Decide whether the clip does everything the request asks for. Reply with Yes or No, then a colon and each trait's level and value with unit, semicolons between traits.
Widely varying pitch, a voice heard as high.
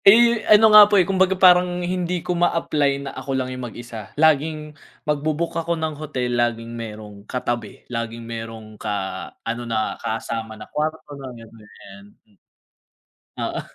No: wide, 6.9 semitones; low, 130 Hz